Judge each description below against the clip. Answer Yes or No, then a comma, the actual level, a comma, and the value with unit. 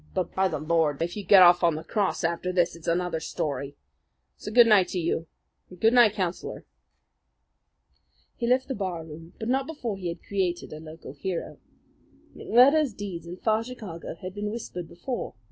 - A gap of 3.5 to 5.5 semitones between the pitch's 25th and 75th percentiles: Yes, average, 4.4 semitones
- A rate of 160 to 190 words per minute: Yes, average, 175 wpm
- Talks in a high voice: No, medium, 180 Hz